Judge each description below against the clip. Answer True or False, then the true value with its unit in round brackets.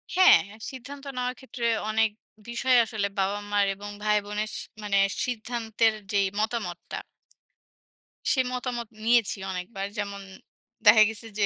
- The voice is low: False (220 Hz)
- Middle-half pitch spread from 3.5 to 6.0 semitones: False (2.7 semitones)